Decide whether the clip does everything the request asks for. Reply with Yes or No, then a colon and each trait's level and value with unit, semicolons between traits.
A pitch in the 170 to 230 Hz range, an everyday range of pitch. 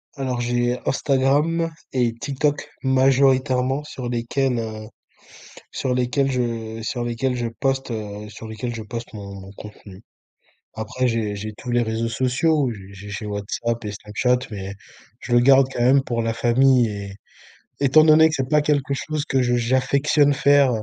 No: low, 125 Hz; average, 3.3 semitones